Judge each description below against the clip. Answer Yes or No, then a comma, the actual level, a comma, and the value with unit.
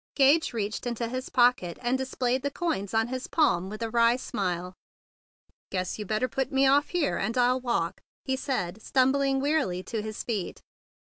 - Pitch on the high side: Yes, high, 245 Hz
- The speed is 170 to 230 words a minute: Yes, average, 180 wpm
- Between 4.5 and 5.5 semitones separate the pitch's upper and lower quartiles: No, average, 4.1 semitones